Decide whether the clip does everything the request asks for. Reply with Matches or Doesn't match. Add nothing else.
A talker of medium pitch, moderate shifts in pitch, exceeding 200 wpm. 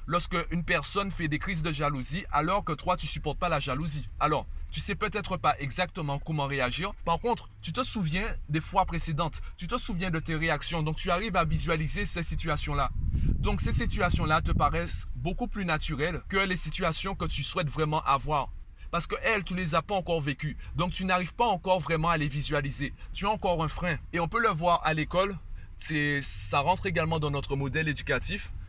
Matches